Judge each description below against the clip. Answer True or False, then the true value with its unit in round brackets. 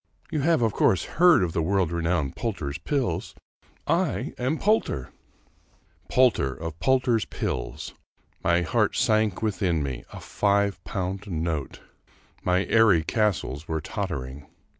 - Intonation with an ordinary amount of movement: False (6.3 semitones)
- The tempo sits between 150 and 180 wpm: False (140 wpm)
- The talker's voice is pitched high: False (95 Hz)